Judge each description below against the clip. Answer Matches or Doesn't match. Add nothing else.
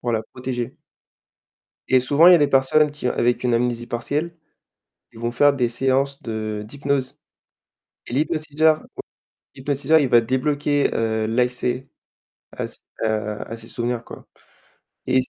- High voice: Doesn't match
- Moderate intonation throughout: Matches